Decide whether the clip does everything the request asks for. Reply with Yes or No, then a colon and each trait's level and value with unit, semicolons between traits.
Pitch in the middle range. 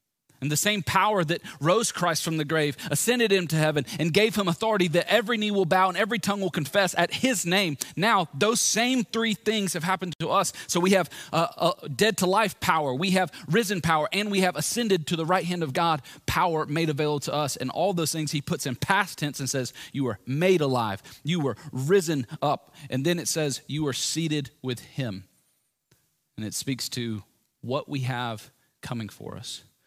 Yes: medium, 165 Hz